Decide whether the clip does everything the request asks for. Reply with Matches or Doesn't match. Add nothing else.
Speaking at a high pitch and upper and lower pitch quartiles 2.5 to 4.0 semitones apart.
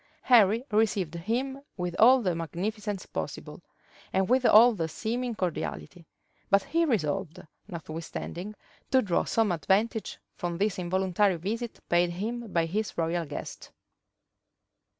Doesn't match